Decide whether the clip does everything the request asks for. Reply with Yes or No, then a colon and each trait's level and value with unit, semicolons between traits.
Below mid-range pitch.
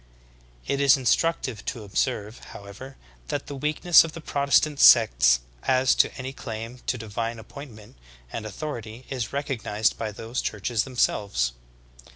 Yes: low, 120 Hz